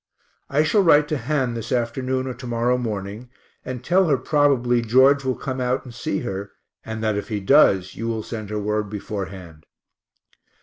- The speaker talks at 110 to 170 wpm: No, average, 185 wpm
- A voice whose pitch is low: Yes, low, 120 Hz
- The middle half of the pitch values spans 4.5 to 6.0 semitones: No, average, 3.8 semitones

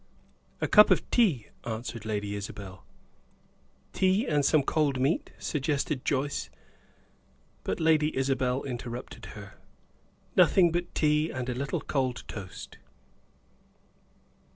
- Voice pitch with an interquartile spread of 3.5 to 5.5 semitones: Yes, average, 4.1 semitones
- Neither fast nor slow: No, slow, 110 wpm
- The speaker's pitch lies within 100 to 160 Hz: Yes, low, 135 Hz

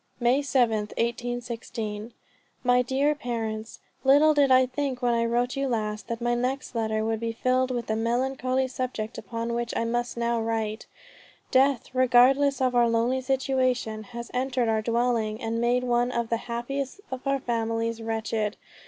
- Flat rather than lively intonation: Yes, narrow, 2.1 semitones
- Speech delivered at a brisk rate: No, average, 160 wpm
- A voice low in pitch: No, high, 240 Hz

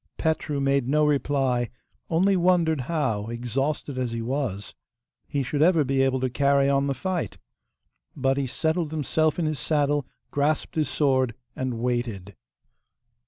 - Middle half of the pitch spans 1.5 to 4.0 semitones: Yes, average, 3.3 semitones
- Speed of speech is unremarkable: Yes, average, 150 wpm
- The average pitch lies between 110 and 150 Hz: Yes, medium, 140 Hz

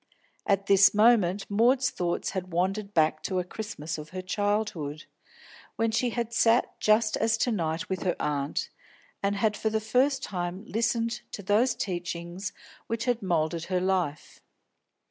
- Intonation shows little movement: No, average, 4.2 semitones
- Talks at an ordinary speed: Yes, average, 160 wpm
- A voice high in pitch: Yes, high, 200 Hz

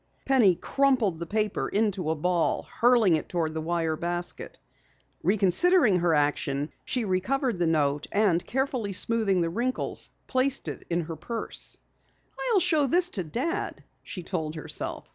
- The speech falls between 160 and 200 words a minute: No, average, 150 wpm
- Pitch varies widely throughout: Yes, wide, 6.8 semitones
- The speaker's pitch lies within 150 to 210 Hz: Yes, high, 190 Hz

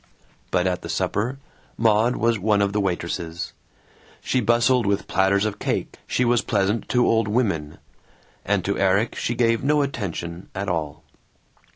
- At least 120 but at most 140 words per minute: No, average, 160 wpm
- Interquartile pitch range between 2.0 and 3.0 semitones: No, average, 3.7 semitones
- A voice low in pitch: Yes, low, 105 Hz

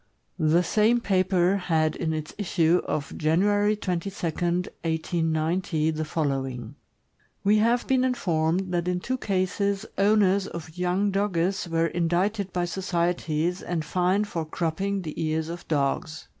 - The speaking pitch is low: No, medium, 175 Hz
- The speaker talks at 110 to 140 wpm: Yes, slow, 135 wpm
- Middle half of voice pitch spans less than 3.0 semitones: No, average, 3.5 semitones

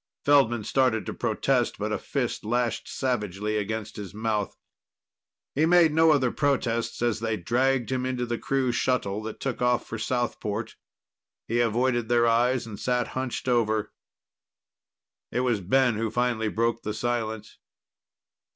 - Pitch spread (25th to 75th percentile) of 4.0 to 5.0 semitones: No, narrow, 2.6 semitones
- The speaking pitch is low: Yes, low, 120 Hz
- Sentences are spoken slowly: No, average, 150 wpm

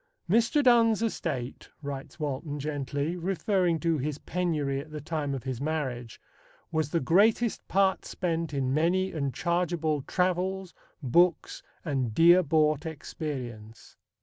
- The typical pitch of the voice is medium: Yes, medium, 155 Hz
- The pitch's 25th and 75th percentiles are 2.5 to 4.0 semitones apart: No, average, 4.4 semitones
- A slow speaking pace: Yes, slow, 130 wpm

